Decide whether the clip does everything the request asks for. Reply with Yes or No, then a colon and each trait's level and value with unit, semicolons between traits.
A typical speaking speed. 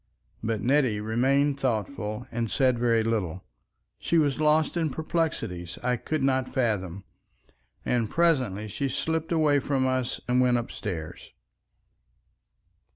No: slow, 125 wpm